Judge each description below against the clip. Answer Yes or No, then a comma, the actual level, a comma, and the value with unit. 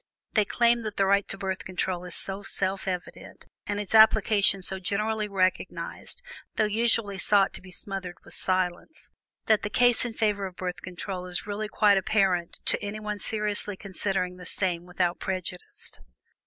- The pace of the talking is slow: No, average, 170 wpm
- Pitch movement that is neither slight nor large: No, narrow, 2.3 semitones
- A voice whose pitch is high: Yes, high, 195 Hz